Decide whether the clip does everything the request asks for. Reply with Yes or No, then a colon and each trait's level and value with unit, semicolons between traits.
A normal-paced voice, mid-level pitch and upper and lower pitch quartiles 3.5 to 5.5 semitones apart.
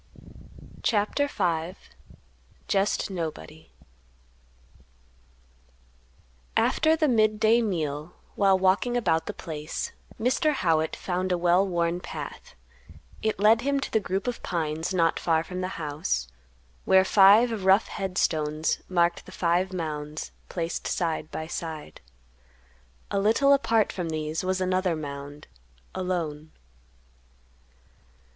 No: slow, 115 wpm; medium, 180 Hz; average, 4.2 semitones